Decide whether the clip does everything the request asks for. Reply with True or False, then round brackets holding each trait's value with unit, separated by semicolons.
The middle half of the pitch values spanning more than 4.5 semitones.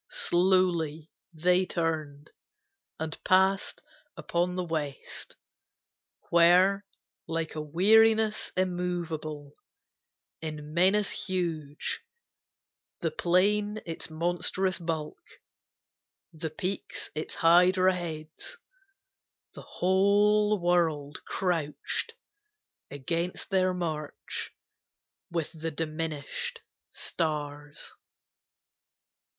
False (3.1 semitones)